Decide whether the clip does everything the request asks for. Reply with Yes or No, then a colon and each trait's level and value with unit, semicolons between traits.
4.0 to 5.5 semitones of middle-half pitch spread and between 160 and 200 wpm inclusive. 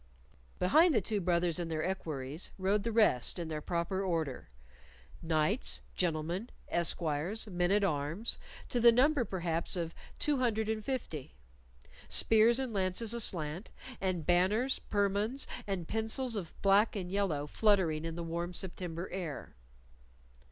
No: average, 4.7 semitones; average, 140 wpm